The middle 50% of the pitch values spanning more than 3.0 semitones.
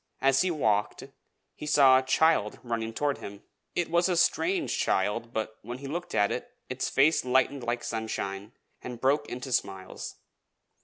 Yes: average, 4.8 semitones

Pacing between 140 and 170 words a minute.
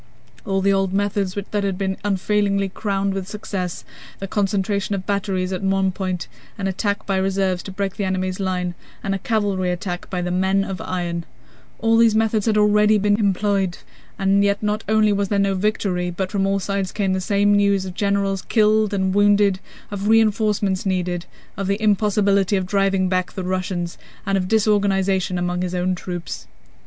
No: average, 180 wpm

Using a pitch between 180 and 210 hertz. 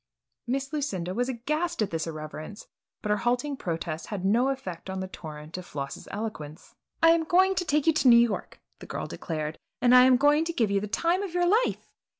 No: high, 235 Hz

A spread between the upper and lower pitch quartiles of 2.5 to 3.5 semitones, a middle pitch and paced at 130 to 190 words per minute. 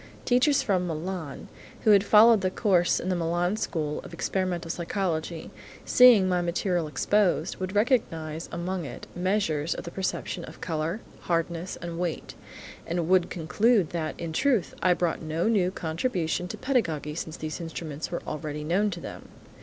Yes: average, 3.1 semitones; medium, 175 Hz; average, 160 wpm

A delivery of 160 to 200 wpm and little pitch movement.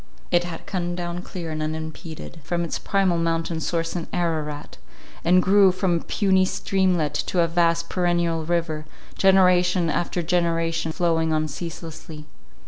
No: average, 145 wpm; narrow, 1.7 semitones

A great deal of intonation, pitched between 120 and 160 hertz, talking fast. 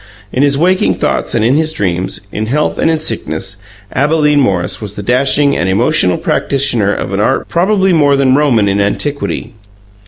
No: wide, 6.5 semitones; low, 135 Hz; average, 180 wpm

